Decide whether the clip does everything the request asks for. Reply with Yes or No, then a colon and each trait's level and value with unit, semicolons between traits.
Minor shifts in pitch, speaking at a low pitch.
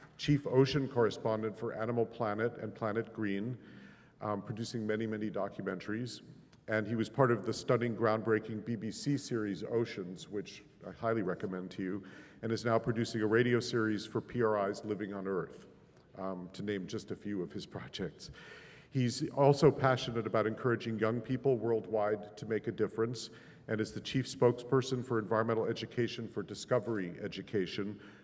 Yes: narrow, 2.2 semitones; low, 115 Hz